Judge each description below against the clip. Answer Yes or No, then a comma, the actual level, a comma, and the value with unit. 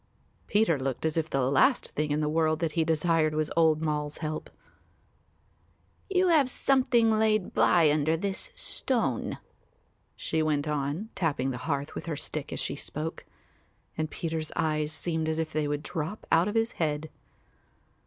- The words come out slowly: No, average, 165 wpm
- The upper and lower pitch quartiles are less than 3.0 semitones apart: Yes, narrow, 2.4 semitones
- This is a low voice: No, medium, 160 Hz